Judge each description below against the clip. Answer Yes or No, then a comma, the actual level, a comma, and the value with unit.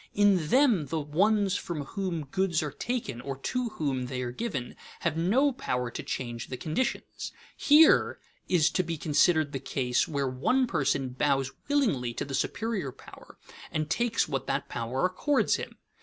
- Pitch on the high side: No, medium, 155 Hz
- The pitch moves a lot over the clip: Yes, wide, 7.3 semitones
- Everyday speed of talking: Yes, average, 170 wpm